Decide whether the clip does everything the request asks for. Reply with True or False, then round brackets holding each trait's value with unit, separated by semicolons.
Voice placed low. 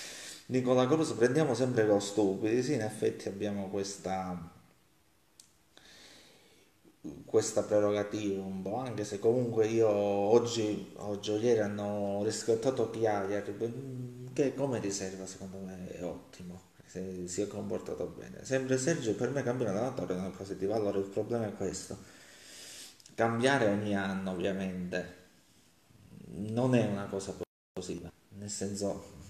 True (100 Hz)